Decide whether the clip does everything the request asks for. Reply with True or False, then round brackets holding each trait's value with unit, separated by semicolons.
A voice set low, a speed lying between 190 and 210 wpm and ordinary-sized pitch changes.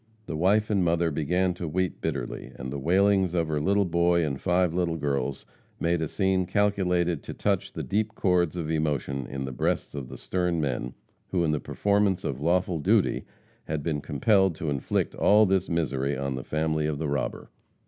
True (85 Hz; 195 wpm; 4.2 semitones)